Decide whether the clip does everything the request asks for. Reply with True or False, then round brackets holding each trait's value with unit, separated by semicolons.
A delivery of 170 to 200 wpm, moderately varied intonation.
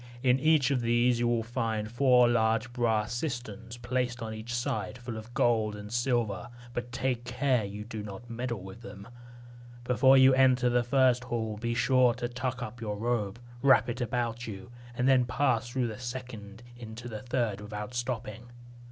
False (180 wpm; 2.1 semitones)